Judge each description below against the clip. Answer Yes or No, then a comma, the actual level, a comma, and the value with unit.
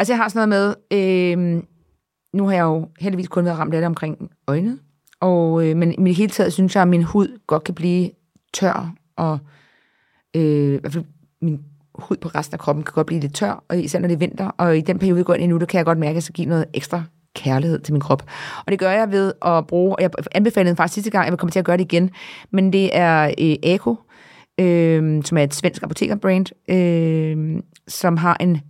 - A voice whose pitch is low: No, medium, 175 Hz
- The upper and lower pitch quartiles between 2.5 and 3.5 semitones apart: Yes, average, 2.8 semitones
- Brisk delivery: Yes, fast, 240 wpm